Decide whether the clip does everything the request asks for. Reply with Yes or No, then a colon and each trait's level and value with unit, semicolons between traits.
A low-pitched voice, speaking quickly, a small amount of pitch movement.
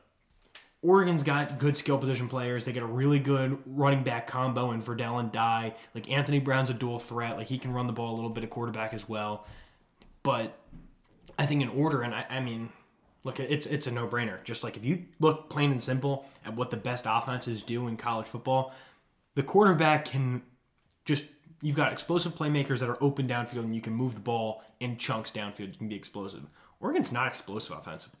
No: low, 125 Hz; fast, 210 wpm; average, 3.3 semitones